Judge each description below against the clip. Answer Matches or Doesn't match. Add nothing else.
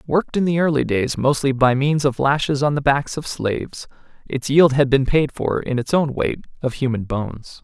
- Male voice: Matches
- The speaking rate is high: Matches